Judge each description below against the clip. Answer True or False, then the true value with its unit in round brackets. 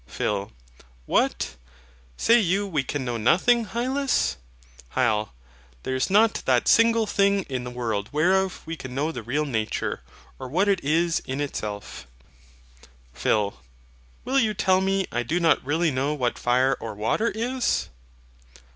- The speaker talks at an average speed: True (150 wpm)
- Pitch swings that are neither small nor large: False (8.3 semitones)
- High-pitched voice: False (150 Hz)